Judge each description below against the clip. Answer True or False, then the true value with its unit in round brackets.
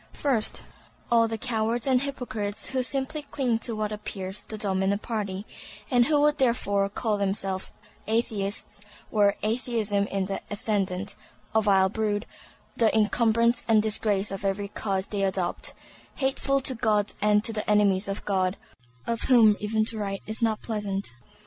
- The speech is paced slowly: False (155 wpm)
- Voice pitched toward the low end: False (215 Hz)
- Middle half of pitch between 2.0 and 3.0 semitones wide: True (2.6 semitones)